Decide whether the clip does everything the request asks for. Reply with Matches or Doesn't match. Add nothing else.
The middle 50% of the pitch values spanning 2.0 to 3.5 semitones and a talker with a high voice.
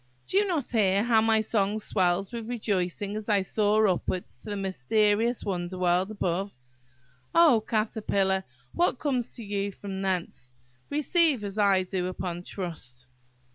Matches